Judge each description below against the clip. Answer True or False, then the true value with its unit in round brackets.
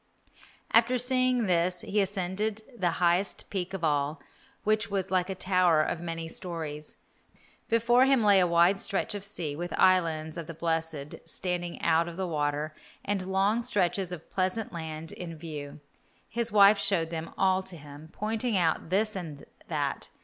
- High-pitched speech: False (180 Hz)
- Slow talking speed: False (165 wpm)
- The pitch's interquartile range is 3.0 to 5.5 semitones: True (3.8 semitones)